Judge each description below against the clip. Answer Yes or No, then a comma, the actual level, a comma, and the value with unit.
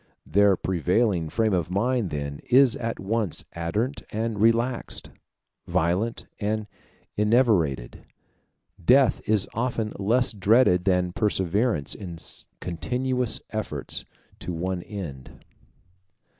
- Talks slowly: Yes, slow, 100 wpm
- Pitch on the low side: Yes, low, 105 Hz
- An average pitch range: Yes, average, 4.6 semitones